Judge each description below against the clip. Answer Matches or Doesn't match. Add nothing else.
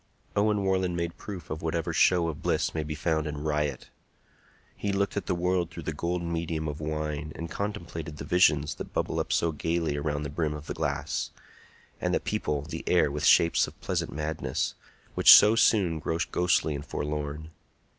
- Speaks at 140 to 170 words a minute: Doesn't match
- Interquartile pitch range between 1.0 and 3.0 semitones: Matches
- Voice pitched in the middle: Doesn't match